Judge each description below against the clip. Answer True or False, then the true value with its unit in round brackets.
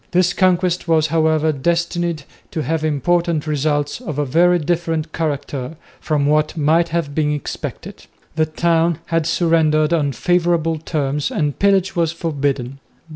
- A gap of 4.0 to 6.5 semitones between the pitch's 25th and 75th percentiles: False (2.4 semitones)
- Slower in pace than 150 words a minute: True (140 wpm)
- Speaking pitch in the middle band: True (160 Hz)